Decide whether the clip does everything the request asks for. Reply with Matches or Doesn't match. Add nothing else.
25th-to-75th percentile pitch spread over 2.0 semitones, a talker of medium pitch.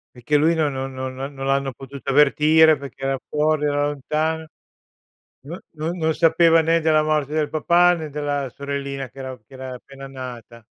Matches